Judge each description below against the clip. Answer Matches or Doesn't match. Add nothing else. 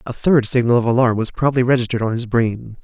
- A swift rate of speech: Matches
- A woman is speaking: Doesn't match